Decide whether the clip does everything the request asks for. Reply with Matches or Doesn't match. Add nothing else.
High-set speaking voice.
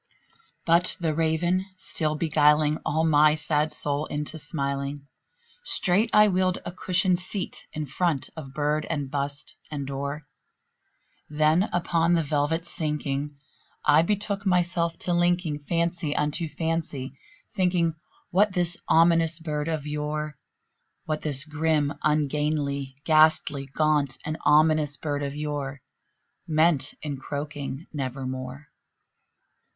Doesn't match